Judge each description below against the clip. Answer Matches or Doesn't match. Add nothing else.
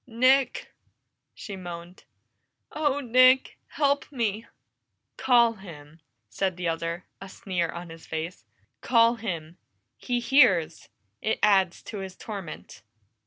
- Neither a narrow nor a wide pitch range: Doesn't match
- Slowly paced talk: Matches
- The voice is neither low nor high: Doesn't match